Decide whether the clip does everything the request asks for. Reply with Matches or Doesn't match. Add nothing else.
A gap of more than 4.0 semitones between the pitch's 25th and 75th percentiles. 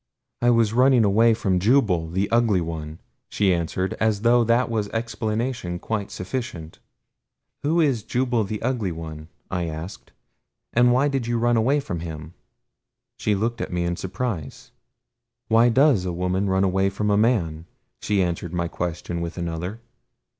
Matches